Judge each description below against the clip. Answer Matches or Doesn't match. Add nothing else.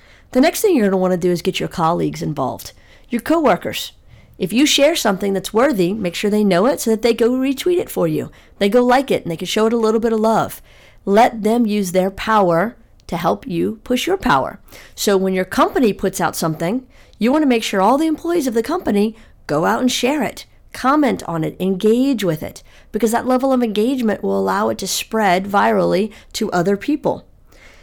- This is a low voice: Doesn't match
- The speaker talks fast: Matches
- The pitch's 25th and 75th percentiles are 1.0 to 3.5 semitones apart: Doesn't match